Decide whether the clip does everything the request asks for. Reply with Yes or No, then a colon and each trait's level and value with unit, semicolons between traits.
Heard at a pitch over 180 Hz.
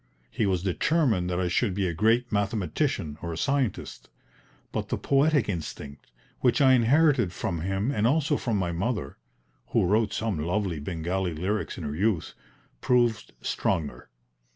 No: low, 100 Hz